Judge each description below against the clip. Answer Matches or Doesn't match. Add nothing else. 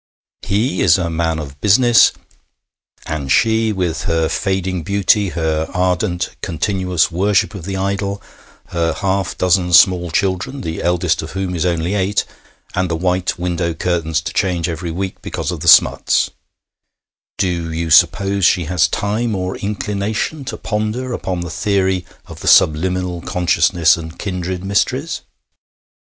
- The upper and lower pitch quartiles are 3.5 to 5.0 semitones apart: Doesn't match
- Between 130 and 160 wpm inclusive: Matches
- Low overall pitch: Matches